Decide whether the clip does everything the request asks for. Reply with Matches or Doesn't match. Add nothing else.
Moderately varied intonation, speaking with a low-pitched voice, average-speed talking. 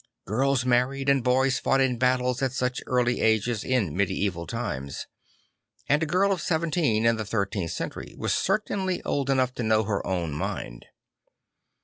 Matches